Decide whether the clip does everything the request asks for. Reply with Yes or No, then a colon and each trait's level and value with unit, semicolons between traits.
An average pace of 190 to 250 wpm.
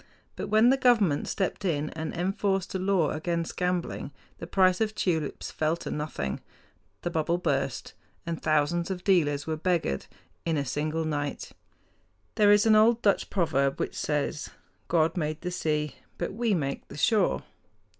No: average, 165 wpm